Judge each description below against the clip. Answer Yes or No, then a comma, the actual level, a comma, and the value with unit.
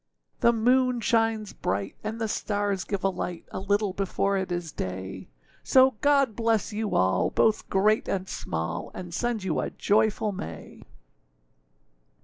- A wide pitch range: No, average, 3.8 semitones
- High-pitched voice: Yes, high, 205 Hz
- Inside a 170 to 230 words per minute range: No, average, 150 wpm